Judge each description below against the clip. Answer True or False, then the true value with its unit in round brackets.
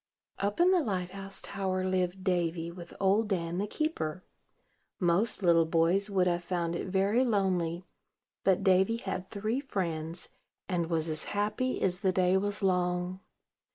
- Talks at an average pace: True (155 wpm)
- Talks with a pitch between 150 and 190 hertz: True (185 Hz)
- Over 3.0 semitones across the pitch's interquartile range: False (2.4 semitones)